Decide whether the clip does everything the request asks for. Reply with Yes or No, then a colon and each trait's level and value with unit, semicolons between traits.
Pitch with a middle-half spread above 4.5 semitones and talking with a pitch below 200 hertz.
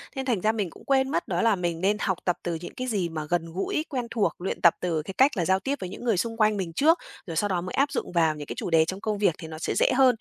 Yes: average, 5.2 semitones; high, 190 Hz